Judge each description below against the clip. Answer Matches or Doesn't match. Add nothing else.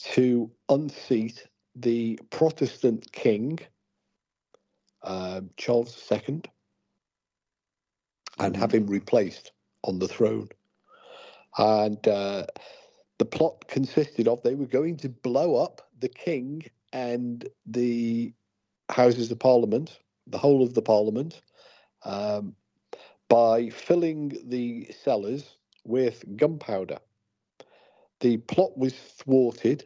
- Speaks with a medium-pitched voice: Doesn't match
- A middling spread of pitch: Matches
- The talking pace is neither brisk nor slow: Doesn't match